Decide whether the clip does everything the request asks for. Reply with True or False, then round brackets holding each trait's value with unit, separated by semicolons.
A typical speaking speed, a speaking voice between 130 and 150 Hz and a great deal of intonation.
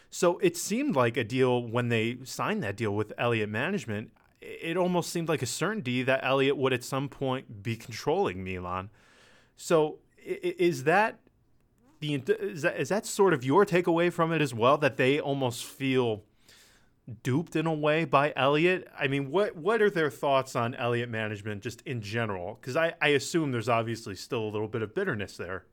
True (190 wpm; 135 Hz; 6.0 semitones)